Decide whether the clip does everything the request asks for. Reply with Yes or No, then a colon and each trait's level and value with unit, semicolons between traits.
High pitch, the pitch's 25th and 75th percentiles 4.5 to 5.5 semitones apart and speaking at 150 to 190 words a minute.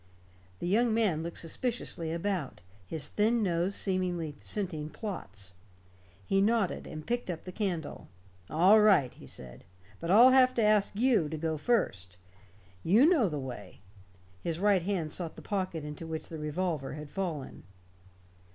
No: medium, 175 Hz; average, 5.2 semitones; average, 155 wpm